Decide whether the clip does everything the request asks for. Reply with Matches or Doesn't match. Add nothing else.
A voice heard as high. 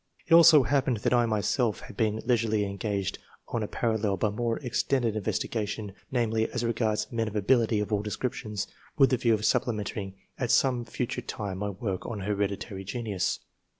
Doesn't match